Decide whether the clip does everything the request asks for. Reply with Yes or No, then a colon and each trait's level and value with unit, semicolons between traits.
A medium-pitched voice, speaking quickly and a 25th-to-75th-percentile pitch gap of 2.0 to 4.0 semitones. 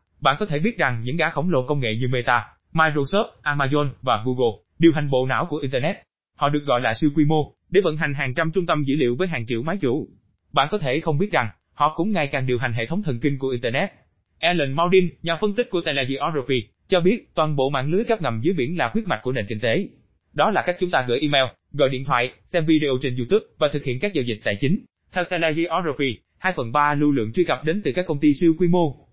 No: medium, 150 Hz; fast, 260 wpm; average, 4.8 semitones